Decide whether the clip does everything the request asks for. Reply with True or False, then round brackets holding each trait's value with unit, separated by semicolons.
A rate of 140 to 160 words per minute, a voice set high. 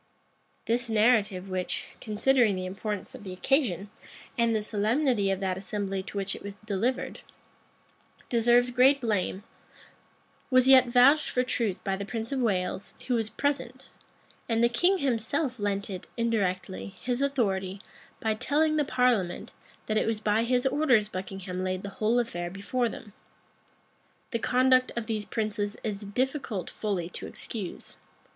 True (155 wpm; 220 Hz)